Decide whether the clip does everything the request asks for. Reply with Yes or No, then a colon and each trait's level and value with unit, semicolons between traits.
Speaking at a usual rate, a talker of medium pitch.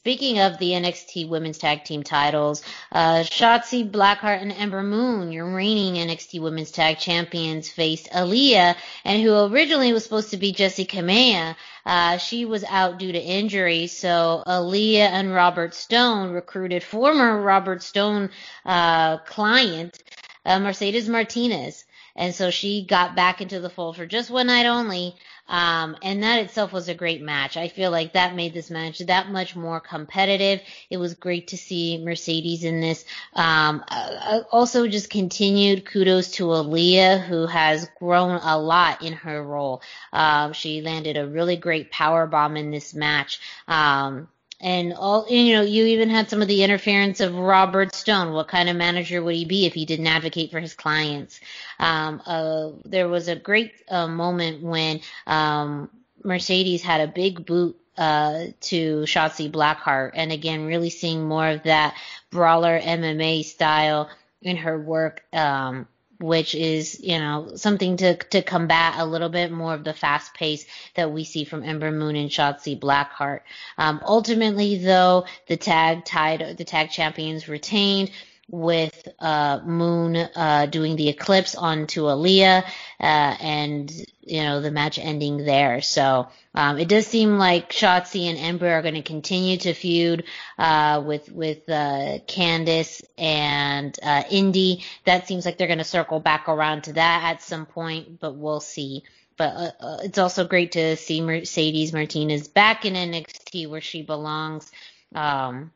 Yes: average, 165 wpm; medium, 170 Hz